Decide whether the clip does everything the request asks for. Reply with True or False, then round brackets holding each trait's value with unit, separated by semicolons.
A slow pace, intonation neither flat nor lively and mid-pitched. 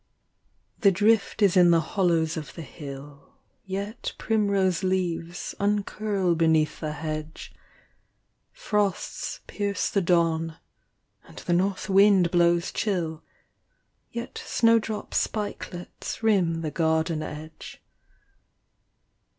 True (100 wpm; 3.9 semitones; 175 Hz)